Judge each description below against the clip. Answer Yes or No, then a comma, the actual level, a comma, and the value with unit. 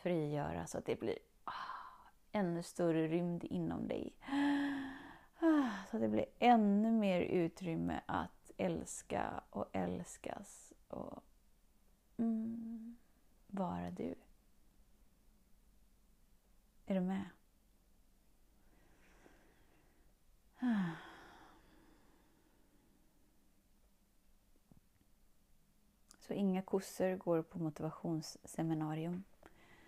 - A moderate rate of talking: No, slow, 70 wpm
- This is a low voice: No, high, 190 Hz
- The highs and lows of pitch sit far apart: Yes, wide, 5.7 semitones